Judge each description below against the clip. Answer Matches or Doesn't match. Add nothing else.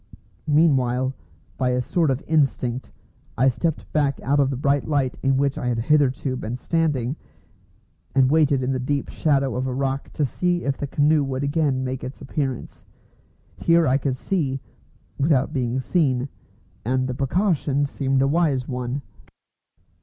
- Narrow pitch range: Matches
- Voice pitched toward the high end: Doesn't match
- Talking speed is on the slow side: Doesn't match